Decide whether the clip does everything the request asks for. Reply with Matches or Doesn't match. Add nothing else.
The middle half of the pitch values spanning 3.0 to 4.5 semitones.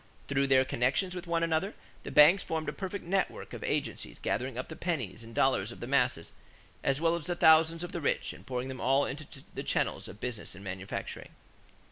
Doesn't match